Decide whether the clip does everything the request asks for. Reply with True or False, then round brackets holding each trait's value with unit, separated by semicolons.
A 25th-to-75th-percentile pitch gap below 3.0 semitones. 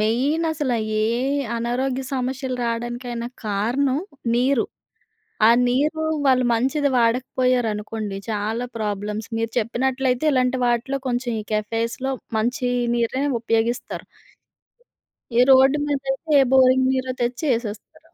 True (2.5 semitones)